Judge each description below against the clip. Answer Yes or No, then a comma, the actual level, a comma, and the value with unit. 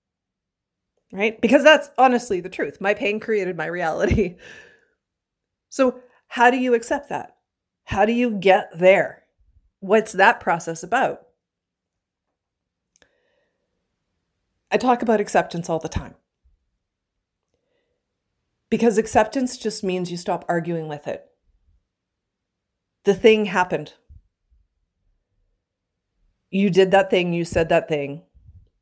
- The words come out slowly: Yes, slow, 110 wpm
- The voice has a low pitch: No, high, 190 Hz